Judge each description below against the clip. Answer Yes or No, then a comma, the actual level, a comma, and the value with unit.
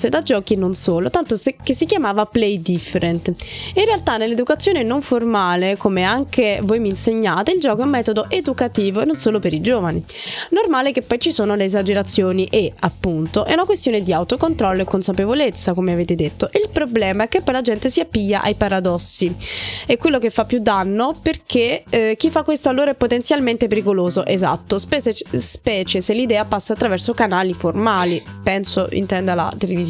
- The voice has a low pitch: No, high, 220 Hz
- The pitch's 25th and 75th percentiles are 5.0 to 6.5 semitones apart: Yes, average, 5.3 semitones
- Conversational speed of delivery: No, fast, 185 wpm